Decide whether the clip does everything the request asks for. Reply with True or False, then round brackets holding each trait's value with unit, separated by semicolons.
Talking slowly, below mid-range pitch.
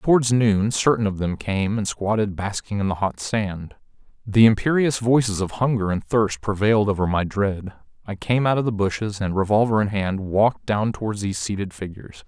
False (195 wpm; 105 Hz)